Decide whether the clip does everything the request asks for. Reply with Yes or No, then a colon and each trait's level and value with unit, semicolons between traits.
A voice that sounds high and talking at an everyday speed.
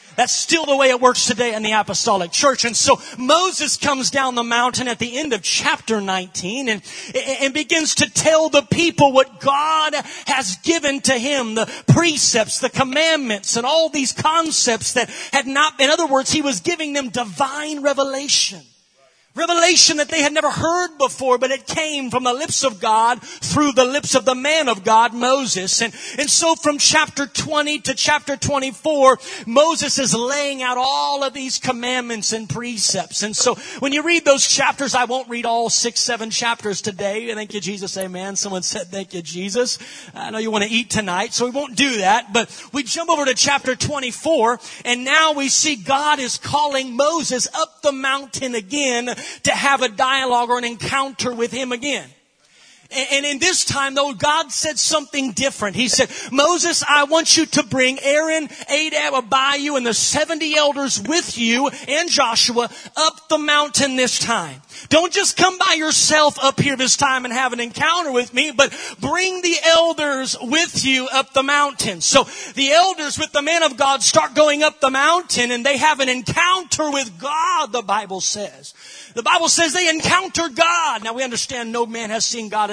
Yes: very high, 270 Hz; average, 190 wpm